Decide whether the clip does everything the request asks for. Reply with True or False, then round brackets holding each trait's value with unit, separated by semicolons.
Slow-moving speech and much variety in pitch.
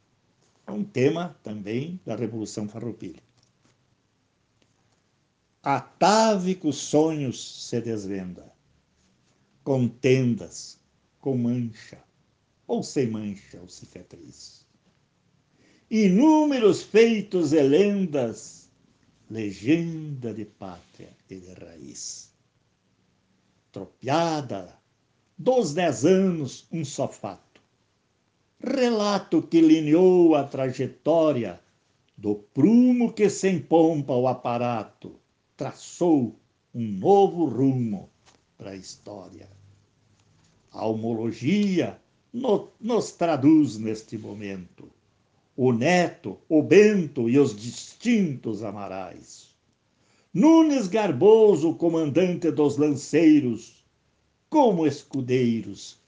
True (80 wpm; 7.8 semitones)